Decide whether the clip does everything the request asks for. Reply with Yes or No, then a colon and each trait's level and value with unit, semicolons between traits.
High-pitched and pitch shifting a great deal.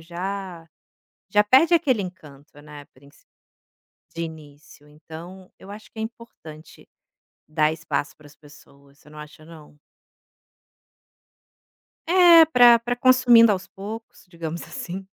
No: medium, 170 Hz; wide, 6.8 semitones